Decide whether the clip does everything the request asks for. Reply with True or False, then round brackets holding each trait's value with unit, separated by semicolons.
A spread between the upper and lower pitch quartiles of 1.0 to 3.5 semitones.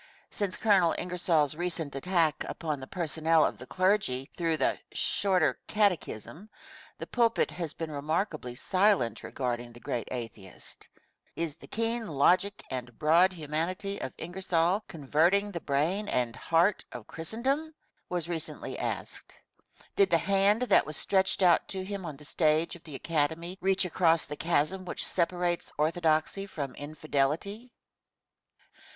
False (4.4 semitones)